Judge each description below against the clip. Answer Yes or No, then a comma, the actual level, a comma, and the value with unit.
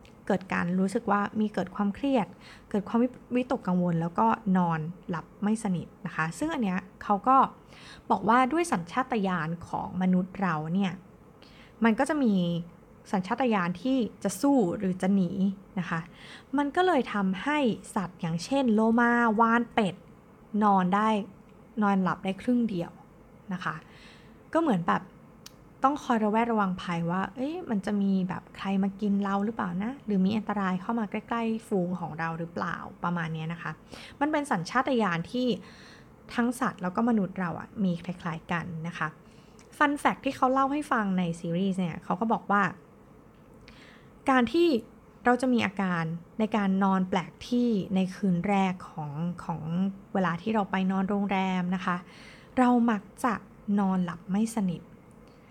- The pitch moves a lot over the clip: No, average, 4.2 semitones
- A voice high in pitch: Yes, high, 200 Hz